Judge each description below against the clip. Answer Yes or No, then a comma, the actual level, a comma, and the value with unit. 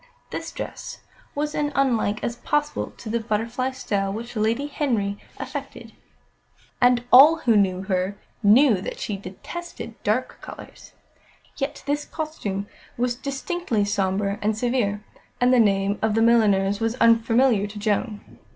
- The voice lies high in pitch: Yes, high, 225 Hz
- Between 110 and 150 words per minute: Yes, average, 140 wpm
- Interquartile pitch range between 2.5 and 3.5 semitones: No, average, 4.1 semitones